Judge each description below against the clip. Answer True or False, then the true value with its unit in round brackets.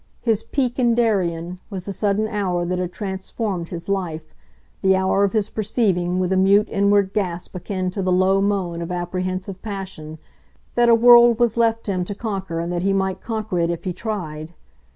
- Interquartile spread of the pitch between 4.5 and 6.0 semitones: False (2.9 semitones)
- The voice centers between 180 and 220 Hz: True (190 Hz)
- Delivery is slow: False (195 wpm)